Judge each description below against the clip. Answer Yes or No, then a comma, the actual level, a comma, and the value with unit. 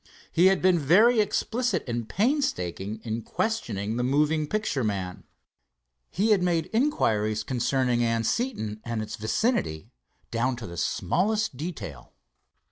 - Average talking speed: No, slow, 125 wpm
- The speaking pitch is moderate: No, low, 130 Hz